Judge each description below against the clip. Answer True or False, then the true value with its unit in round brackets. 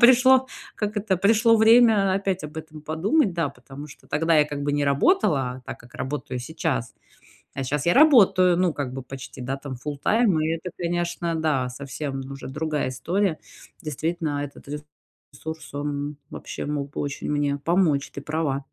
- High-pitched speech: False (155 Hz)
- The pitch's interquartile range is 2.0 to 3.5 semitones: False (4.7 semitones)